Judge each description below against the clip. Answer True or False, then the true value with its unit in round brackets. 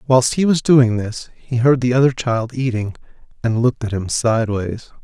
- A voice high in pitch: False (120 Hz)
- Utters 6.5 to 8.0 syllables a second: False (4.9 syllables/s)